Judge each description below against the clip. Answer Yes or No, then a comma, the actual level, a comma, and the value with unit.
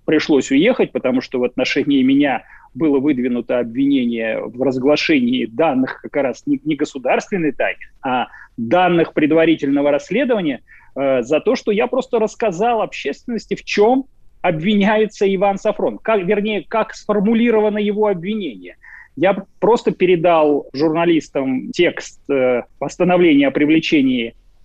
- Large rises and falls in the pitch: Yes, wide, 8.0 semitones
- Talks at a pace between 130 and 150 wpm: No, average, 120 wpm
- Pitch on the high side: Yes, high, 200 Hz